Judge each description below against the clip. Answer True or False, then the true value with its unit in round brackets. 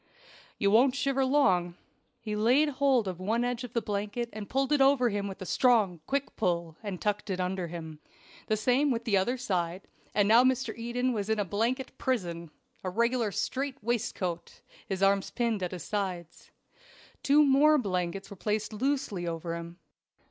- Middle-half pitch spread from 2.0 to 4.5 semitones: False (5.3 semitones)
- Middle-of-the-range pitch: False (215 Hz)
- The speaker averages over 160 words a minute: True (180 wpm)